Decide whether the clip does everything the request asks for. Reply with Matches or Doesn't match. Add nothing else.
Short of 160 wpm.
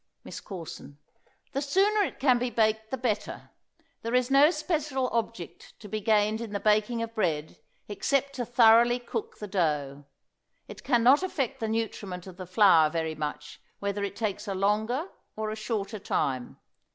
Doesn't match